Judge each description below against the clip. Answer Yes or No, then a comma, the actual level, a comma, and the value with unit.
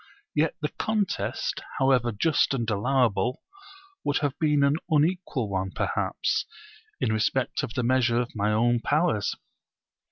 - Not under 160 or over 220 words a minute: No, slow, 135 wpm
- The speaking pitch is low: Yes, low, 130 Hz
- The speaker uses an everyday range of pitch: Yes, average, 4.6 semitones